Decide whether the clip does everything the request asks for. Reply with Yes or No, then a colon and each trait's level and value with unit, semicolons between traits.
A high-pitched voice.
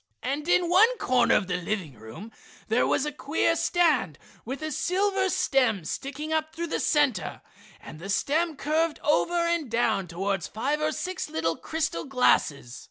Yes: very high, 285 Hz